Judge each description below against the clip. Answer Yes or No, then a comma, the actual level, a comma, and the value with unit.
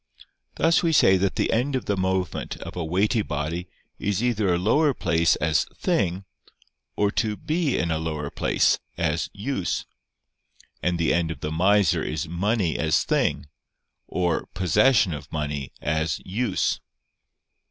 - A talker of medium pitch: No, very low, 90 Hz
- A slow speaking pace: No, average, 150 wpm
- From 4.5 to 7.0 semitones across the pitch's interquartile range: Yes, average, 4.8 semitones